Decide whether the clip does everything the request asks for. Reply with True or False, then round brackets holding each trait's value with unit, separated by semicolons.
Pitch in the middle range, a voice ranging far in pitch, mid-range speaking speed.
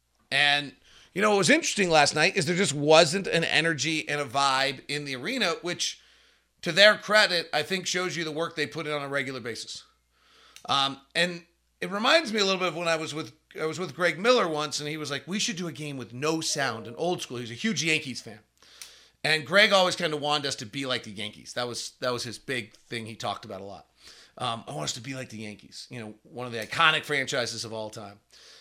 False (150 Hz; 5.7 semitones; 250 wpm)